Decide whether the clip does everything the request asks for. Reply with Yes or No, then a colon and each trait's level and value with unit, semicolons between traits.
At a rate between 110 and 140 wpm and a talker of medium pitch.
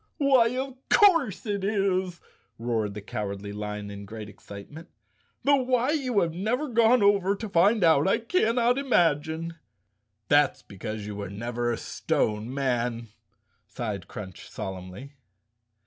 Yes: slow, 135 wpm; medium, 160 Hz